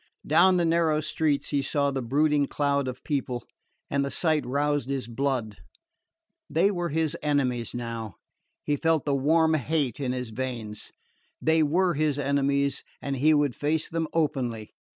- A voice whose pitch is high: No, medium, 140 Hz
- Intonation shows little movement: No, average, 3.2 semitones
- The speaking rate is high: No, average, 160 wpm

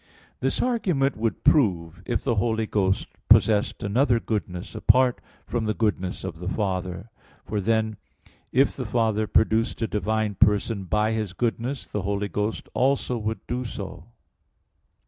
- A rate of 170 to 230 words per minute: No, average, 150 wpm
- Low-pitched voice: Yes, low, 110 Hz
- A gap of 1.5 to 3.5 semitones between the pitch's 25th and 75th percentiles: Yes, average, 2.8 semitones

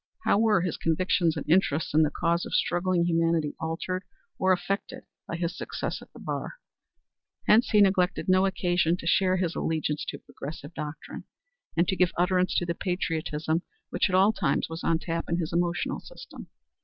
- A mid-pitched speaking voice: Yes, medium, 175 Hz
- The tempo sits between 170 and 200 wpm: Yes, average, 180 wpm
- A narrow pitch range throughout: Yes, narrow, 2.3 semitones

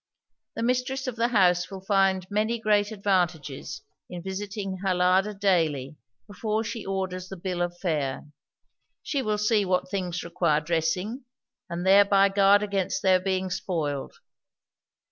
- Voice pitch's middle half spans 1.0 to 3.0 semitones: Yes, average, 2.7 semitones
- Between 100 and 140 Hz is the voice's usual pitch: No, high, 190 Hz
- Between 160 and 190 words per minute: No, average, 145 wpm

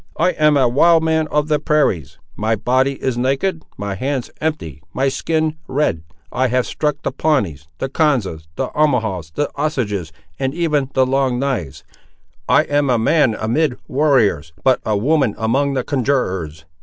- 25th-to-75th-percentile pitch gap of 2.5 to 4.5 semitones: No, wide, 5.4 semitones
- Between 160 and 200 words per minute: Yes, average, 165 wpm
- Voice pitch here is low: Yes, low, 130 Hz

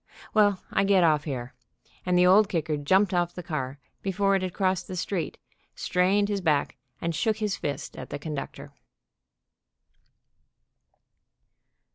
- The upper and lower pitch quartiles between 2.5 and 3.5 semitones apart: No, average, 4.4 semitones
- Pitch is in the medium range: Yes, medium, 180 Hz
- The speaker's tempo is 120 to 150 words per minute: Yes, average, 145 wpm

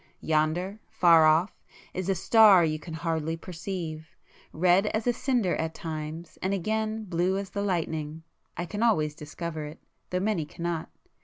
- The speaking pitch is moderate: Yes, medium, 170 Hz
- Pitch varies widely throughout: No, average, 3.7 semitones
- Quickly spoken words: No, average, 155 wpm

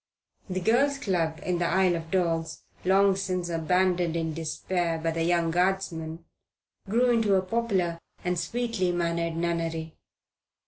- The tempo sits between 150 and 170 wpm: No, average, 140 wpm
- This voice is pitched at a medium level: Yes, medium, 175 Hz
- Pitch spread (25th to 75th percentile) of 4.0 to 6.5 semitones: No, narrow, 2.4 semitones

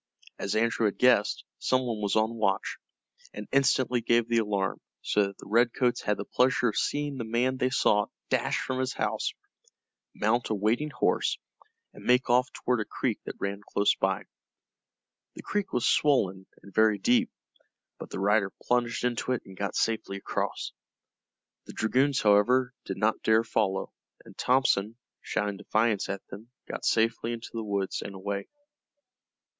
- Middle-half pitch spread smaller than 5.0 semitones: Yes, average, 3.4 semitones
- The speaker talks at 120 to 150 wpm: No, average, 165 wpm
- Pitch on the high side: No, low, 110 Hz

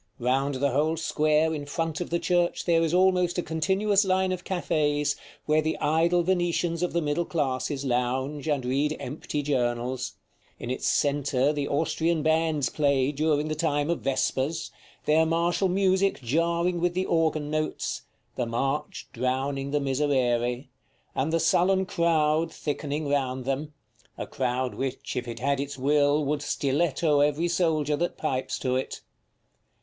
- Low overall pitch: No, medium, 150 Hz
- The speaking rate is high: No, average, 155 wpm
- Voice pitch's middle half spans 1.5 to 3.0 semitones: No, average, 3.5 semitones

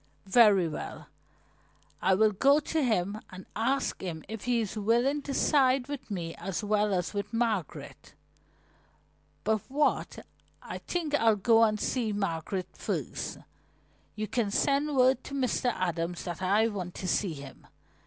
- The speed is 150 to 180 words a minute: Yes, average, 155 wpm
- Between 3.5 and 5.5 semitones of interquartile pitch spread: Yes, average, 5.1 semitones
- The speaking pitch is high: Yes, high, 215 Hz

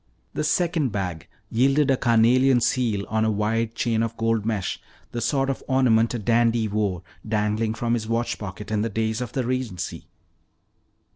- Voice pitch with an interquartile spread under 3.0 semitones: Yes, narrow, 2.4 semitones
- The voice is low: Yes, low, 115 Hz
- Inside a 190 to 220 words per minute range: No, average, 170 wpm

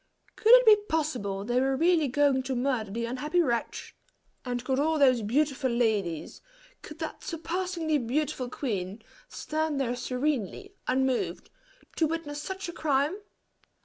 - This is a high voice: Yes, very high, 275 Hz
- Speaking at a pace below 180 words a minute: Yes, average, 145 wpm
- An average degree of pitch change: Yes, average, 4.4 semitones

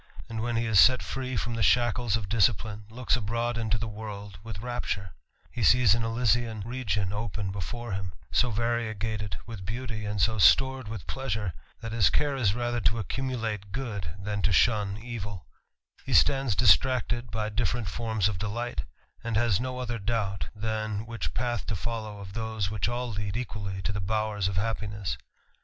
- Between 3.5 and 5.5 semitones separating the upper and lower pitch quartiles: No, average, 2.7 semitones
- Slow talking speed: No, average, 180 wpm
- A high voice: No, low, 110 Hz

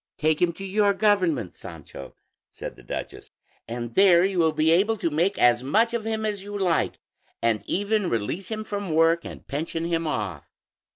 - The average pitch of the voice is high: No, medium, 170 Hz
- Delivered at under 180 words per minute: No, average, 185 wpm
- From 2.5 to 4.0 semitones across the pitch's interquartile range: No, average, 4.9 semitones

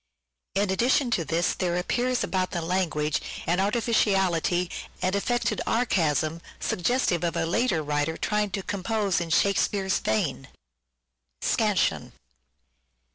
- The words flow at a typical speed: No, slow, 120 wpm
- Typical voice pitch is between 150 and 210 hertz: Yes, medium, 185 Hz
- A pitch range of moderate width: Yes, average, 3.9 semitones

